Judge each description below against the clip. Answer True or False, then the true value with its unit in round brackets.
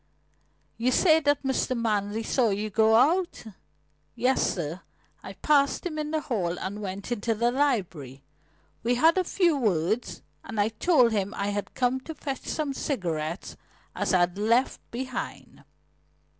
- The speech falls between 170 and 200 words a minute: False (155 wpm)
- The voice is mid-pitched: False (230 Hz)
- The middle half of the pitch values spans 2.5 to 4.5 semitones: False (5.6 semitones)